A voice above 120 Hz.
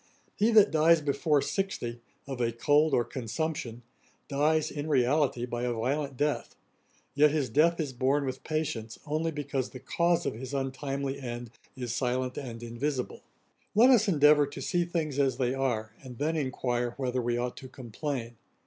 Yes: low, 135 Hz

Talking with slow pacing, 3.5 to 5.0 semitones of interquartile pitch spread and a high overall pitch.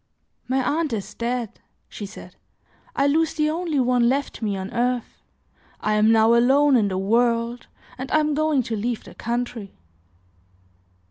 No: average, 160 wpm; average, 4.0 semitones; high, 245 Hz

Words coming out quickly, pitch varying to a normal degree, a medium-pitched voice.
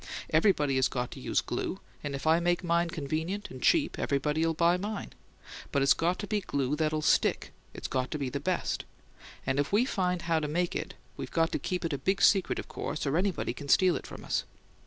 Yes: fast, 220 wpm; average, 4.2 semitones; medium, 165 Hz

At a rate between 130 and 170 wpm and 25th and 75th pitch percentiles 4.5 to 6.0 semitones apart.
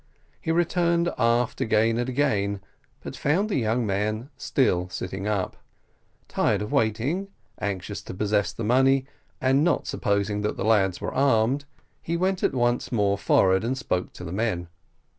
Yes: average, 155 wpm; average, 5.0 semitones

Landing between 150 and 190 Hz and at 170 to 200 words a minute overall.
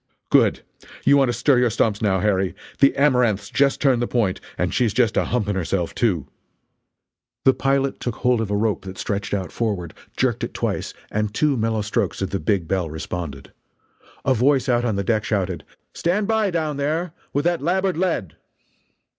No: low, 115 Hz; average, 190 wpm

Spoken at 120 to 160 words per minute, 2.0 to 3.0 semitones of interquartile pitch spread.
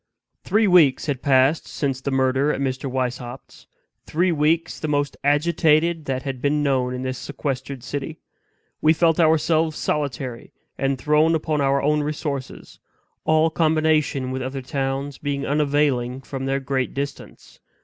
Yes: average, 150 wpm; average, 2.7 semitones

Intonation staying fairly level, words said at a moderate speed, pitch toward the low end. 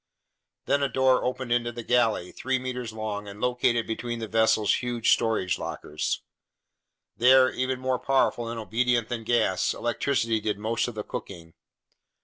Yes: narrow, 2.3 semitones; average, 155 wpm; low, 120 Hz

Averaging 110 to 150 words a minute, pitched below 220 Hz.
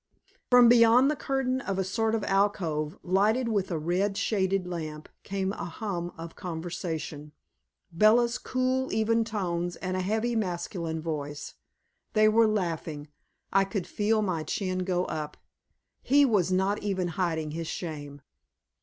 Yes: average, 145 wpm; high, 190 Hz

